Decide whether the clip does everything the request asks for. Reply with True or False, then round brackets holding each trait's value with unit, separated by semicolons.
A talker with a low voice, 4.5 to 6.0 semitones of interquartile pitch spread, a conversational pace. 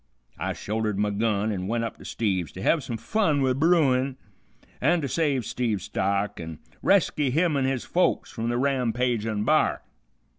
True (120 Hz; 4.8 semitones; 175 wpm)